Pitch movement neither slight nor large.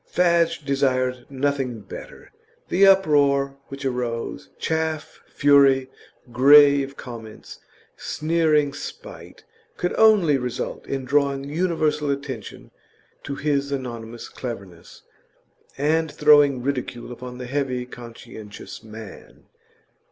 Yes: average, 3.0 semitones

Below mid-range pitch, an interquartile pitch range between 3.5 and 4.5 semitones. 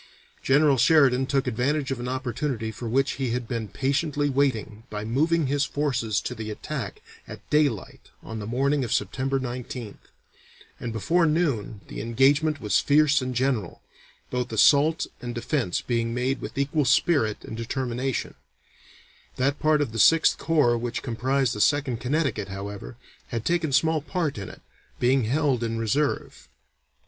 Yes: low, 130 Hz; average, 3.9 semitones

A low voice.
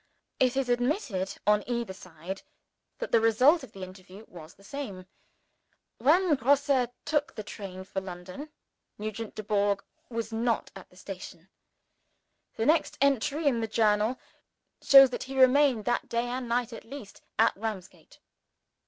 No: high, 225 Hz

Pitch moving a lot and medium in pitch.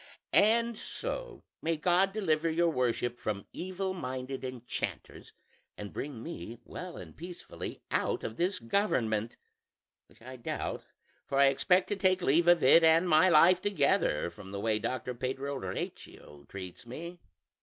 Yes: wide, 7.3 semitones; medium, 150 Hz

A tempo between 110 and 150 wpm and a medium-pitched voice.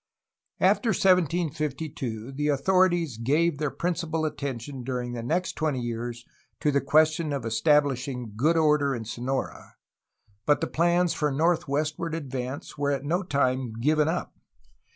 Yes: average, 140 wpm; medium, 145 Hz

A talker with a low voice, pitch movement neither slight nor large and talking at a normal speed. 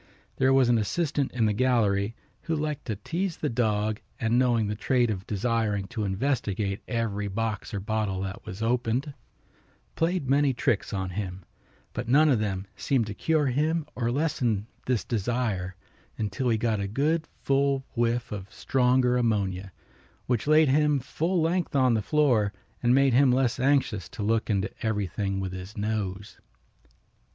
Yes: low, 115 Hz; average, 4.5 semitones; average, 165 wpm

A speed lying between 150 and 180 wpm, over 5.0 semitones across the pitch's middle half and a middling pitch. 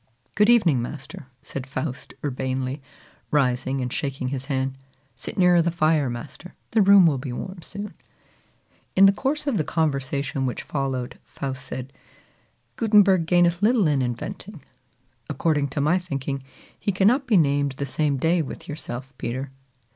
Yes: average, 155 wpm; wide, 5.4 semitones; medium, 145 Hz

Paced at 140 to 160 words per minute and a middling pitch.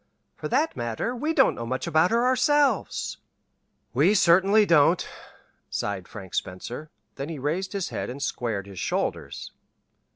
Yes: average, 150 wpm; medium, 165 Hz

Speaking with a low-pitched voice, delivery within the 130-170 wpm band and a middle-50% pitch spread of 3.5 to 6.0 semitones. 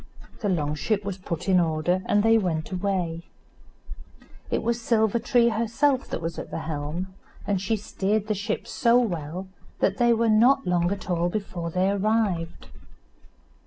No: high, 195 Hz; average, 165 wpm; average, 4.3 semitones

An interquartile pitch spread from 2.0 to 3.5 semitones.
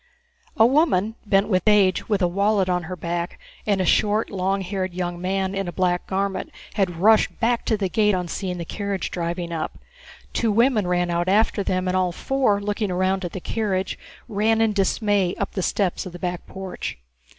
Yes: narrow, 2.5 semitones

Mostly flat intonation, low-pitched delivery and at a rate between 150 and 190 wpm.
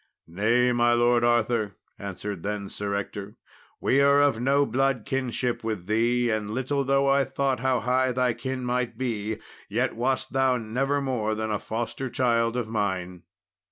No: average, 3.3 semitones; low, 120 Hz; average, 160 wpm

